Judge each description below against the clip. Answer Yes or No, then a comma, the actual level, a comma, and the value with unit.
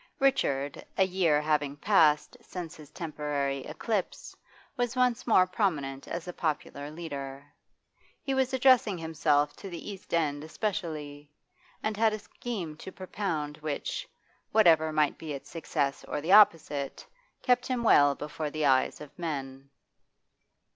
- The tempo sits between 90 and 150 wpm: Yes, average, 140 wpm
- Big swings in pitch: Yes, wide, 5.7 semitones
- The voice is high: No, medium, 160 Hz